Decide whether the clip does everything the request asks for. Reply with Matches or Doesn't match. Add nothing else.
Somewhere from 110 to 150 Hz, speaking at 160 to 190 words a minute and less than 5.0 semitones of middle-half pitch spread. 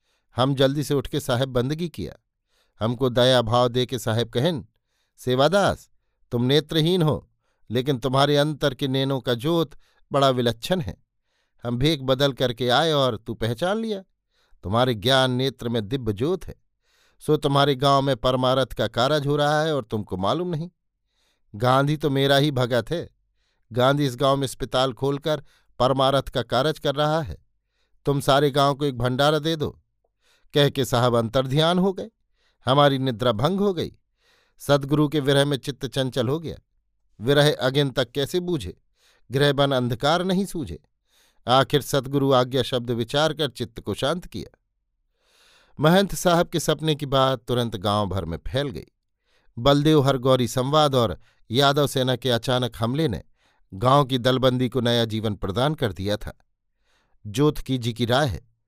Matches